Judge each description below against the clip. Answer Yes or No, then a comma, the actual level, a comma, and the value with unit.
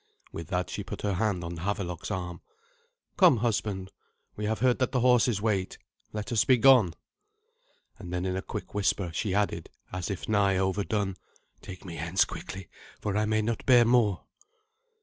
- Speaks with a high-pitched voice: No, low, 100 Hz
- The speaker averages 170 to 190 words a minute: Yes, average, 175 wpm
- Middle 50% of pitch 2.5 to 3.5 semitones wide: Yes, average, 3.0 semitones